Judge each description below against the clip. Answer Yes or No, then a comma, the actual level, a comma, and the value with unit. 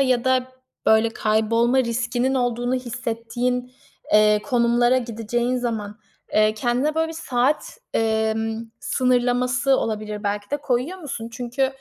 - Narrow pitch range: Yes, narrow, 2.3 semitones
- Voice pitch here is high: Yes, high, 240 Hz